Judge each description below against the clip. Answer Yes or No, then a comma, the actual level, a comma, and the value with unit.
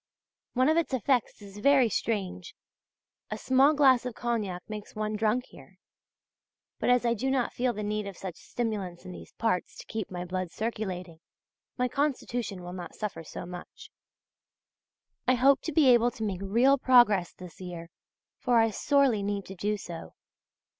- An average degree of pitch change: Yes, average, 5.0 semitones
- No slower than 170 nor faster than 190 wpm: Yes, average, 175 wpm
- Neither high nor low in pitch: No, high, 215 Hz